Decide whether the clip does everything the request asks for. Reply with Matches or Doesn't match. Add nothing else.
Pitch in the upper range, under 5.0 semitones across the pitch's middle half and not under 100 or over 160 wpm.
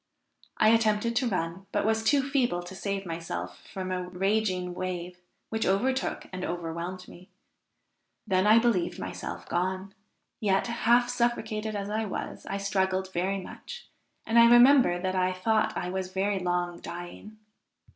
Matches